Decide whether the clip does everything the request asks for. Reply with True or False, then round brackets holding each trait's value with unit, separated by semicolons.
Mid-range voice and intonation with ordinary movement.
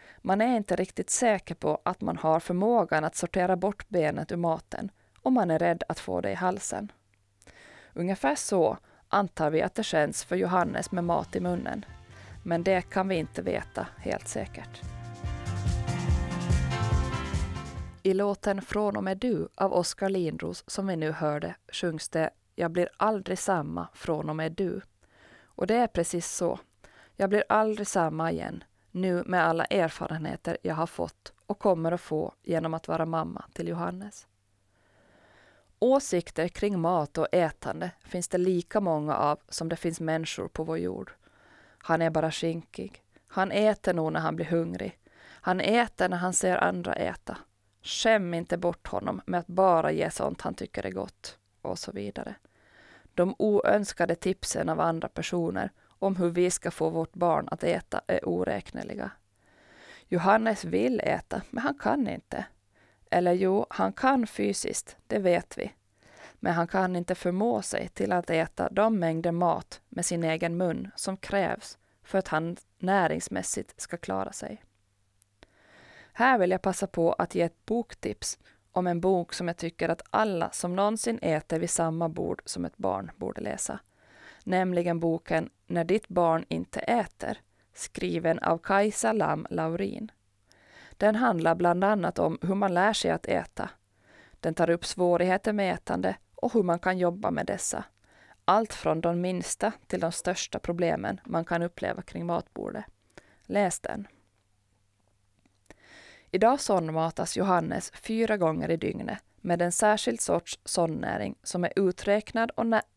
True (175 Hz; 3.8 semitones)